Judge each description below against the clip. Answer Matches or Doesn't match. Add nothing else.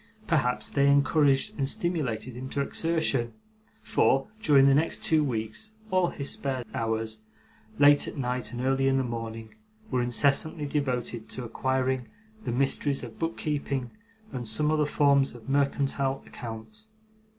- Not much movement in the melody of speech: Doesn't match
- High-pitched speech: Doesn't match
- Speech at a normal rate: Matches